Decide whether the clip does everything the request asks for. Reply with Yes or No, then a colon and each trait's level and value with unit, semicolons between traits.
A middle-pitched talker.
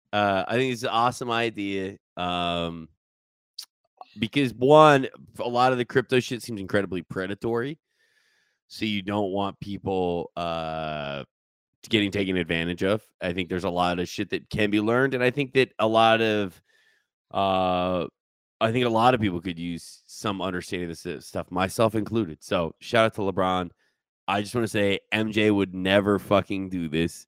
No: low, 100 Hz